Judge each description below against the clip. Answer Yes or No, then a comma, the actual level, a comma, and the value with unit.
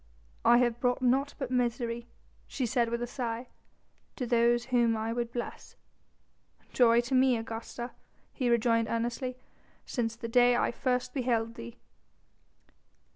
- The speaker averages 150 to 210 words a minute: No, average, 140 wpm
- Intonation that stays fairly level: Yes, narrow, 1.4 semitones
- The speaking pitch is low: No, high, 240 Hz